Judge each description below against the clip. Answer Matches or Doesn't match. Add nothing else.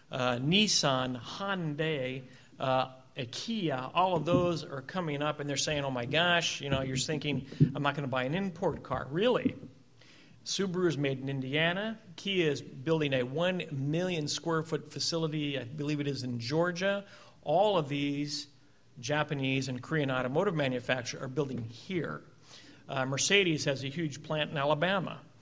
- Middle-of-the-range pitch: Matches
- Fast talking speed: Doesn't match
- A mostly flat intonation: Doesn't match